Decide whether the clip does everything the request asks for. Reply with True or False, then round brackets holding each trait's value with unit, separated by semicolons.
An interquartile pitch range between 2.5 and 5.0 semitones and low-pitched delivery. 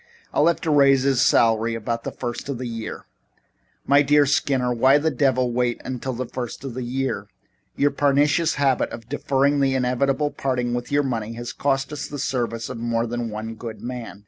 True (2.9 semitones; 130 Hz)